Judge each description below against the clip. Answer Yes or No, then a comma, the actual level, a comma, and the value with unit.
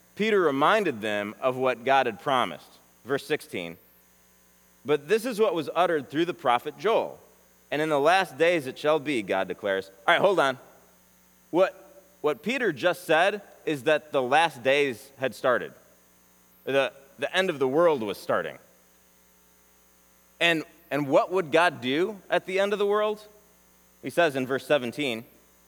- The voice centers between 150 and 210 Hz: No, low, 135 Hz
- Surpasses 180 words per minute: No, average, 165 wpm